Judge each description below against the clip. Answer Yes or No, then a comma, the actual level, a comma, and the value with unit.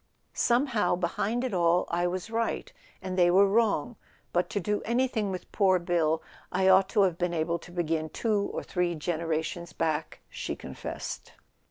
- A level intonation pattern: No, average, 3.4 semitones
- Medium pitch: Yes, medium, 180 Hz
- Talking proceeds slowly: No, average, 170 wpm